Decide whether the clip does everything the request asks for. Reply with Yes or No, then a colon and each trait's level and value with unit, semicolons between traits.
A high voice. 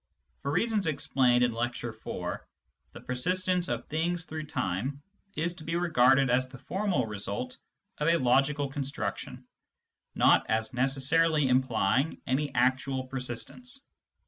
No: low, 135 Hz